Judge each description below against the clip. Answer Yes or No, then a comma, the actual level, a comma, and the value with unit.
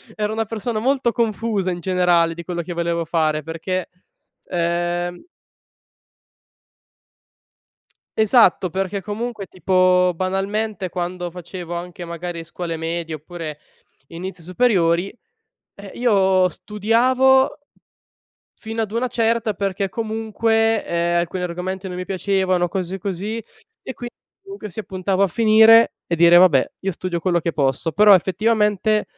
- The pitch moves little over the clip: No, average, 3.9 semitones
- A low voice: No, medium, 185 Hz